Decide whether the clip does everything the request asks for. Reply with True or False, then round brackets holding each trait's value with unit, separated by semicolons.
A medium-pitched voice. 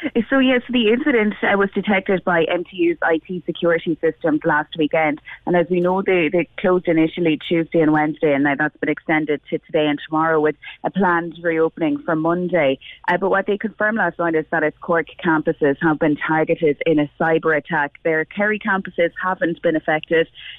True (165 Hz)